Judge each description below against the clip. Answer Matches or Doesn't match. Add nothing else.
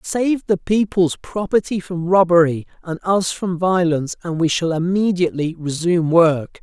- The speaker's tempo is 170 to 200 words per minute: Doesn't match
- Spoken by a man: Matches